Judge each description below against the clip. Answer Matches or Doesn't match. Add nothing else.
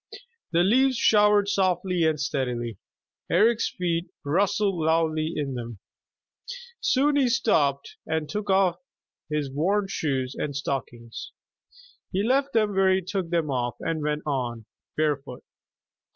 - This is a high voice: Doesn't match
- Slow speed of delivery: Matches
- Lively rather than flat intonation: Matches